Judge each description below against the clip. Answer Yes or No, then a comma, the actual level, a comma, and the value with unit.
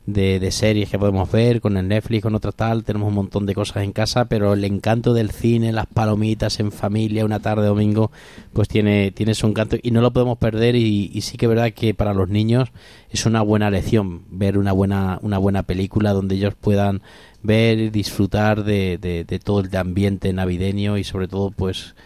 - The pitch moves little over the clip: Yes, narrow, 1.9 semitones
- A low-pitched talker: Yes, low, 105 Hz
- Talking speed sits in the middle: No, fast, 210 wpm